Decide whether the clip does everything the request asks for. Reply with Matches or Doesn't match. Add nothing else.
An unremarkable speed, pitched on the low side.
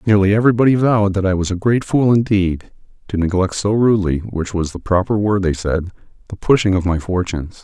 Matches